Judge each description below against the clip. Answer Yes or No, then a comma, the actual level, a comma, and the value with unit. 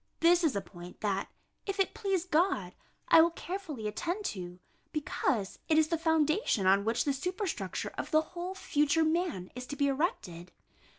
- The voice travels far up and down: Yes, wide, 8.7 semitones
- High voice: Yes, very high, 310 Hz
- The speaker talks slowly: No, average, 175 wpm